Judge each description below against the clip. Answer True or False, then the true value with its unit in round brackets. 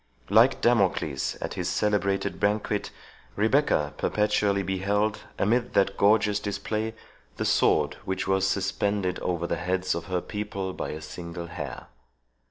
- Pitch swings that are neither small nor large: False (2.3 semitones)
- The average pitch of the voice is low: True (100 Hz)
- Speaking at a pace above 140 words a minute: False (135 wpm)